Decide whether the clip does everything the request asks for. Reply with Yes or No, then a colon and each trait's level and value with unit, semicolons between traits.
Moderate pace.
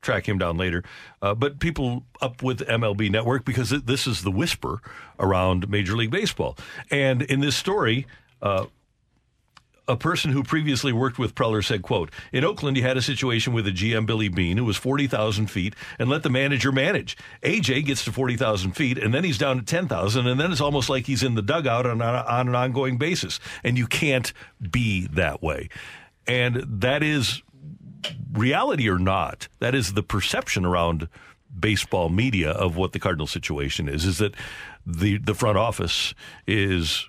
Yes: average, 185 wpm